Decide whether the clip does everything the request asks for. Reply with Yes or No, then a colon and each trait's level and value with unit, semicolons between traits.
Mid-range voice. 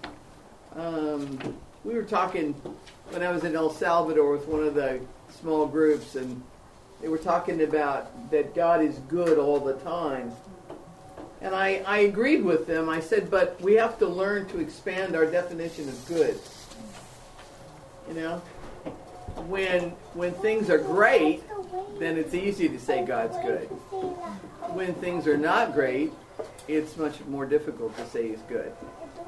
Yes: medium, 170 Hz